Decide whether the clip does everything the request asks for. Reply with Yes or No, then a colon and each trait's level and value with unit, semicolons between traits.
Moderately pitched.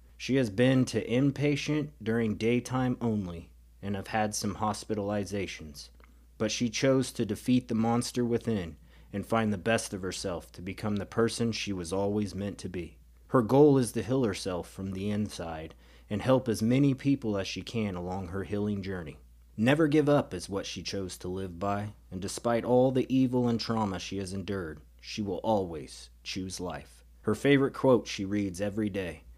No: low, 105 Hz